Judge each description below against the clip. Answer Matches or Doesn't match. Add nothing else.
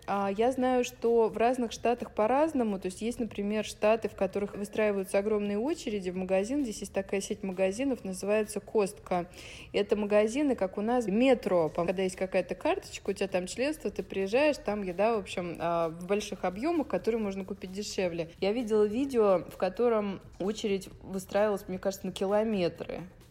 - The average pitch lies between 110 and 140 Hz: Doesn't match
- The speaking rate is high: Matches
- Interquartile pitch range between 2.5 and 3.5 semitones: Matches